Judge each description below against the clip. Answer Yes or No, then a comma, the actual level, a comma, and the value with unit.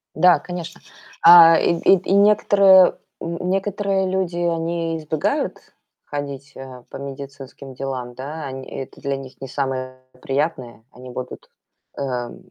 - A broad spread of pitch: No, average, 4.7 semitones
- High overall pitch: No, medium, 145 Hz